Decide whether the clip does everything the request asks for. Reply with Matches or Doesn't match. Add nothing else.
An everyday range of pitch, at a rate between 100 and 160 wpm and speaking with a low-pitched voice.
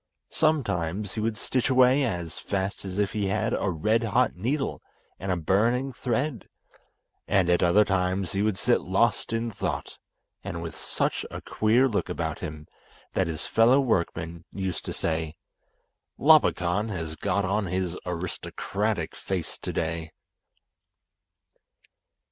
Matches